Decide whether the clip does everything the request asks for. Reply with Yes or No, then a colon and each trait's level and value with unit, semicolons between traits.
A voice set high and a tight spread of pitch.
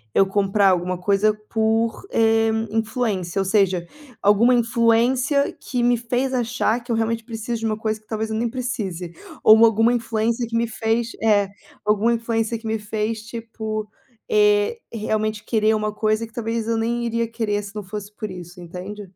Yes: high, 220 Hz; narrow, 1.7 semitones